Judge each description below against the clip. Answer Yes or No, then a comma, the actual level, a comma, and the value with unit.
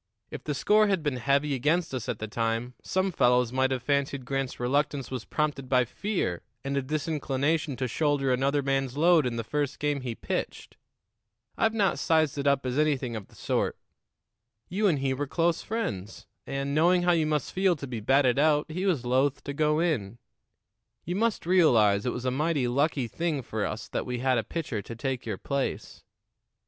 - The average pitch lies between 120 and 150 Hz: Yes, medium, 140 Hz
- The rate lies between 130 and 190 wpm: No, average, 200 wpm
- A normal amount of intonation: Yes, average, 3.7 semitones